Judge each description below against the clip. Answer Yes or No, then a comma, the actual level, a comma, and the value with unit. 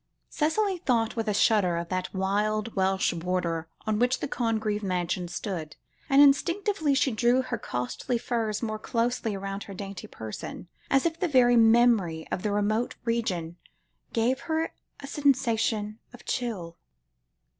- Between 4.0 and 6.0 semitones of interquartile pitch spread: Yes, average, 4.6 semitones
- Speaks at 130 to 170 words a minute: Yes, average, 150 wpm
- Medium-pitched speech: No, high, 220 Hz